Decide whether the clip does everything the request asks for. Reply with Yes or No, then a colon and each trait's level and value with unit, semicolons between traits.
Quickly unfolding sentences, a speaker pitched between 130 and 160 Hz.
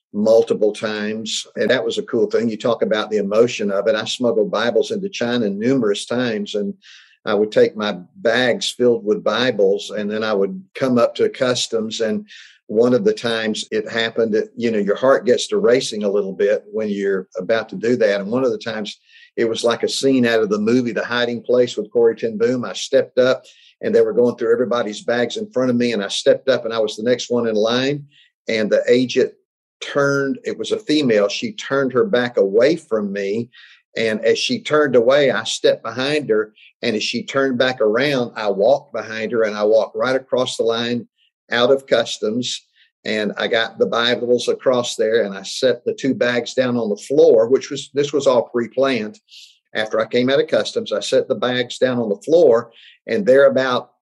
Yes: fast, 215 wpm; medium, 140 Hz